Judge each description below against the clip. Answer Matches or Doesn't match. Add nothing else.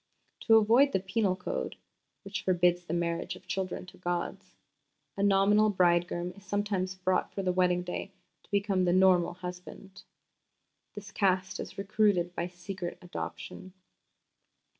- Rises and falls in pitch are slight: Matches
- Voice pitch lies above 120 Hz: Matches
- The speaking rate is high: Doesn't match